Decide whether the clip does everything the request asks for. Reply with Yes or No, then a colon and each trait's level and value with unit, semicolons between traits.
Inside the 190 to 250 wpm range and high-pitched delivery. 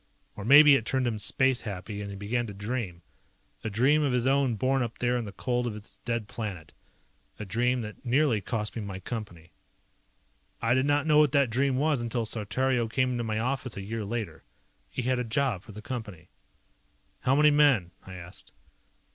No: average, 200 wpm; low, 120 Hz